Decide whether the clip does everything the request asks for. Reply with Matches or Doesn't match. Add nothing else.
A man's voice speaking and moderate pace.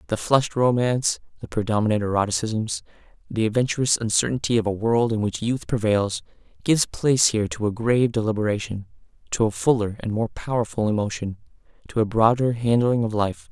Matches